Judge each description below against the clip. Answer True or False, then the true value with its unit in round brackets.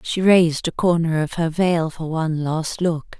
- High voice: False (165 Hz)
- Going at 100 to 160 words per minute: False (205 wpm)